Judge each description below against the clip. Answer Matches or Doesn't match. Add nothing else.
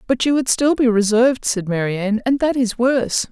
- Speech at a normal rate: Doesn't match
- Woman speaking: Matches